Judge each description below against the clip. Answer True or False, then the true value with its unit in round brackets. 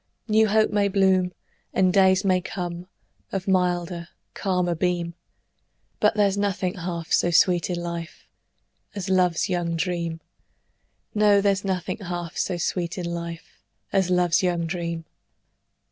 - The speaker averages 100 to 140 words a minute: True (135 wpm)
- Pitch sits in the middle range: True (180 Hz)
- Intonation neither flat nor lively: False (1.9 semitones)